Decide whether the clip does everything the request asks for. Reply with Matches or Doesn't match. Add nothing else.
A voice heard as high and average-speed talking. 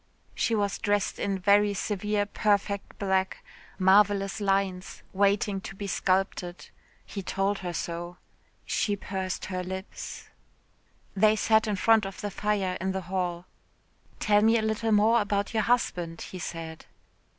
Matches